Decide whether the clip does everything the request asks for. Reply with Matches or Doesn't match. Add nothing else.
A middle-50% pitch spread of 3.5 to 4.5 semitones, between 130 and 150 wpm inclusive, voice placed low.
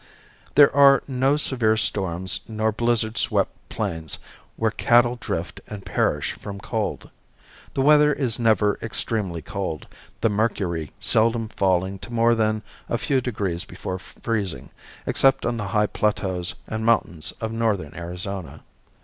Matches